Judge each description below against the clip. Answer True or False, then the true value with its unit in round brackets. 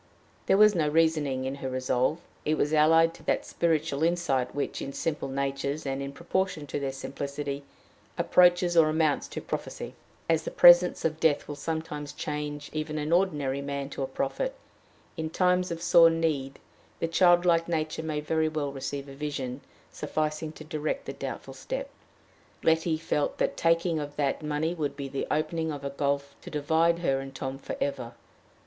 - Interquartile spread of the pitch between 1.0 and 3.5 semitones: True (2.8 semitones)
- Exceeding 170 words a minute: True (180 wpm)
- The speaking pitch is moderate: True (150 Hz)